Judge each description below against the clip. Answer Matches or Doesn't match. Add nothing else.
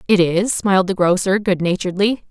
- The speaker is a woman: Matches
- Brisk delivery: Doesn't match